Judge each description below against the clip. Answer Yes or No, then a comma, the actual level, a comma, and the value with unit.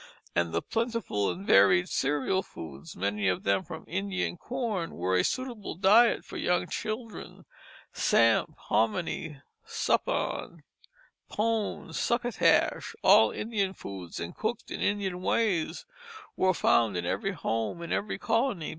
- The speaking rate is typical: No, slow, 130 wpm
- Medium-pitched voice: Yes, medium, 180 Hz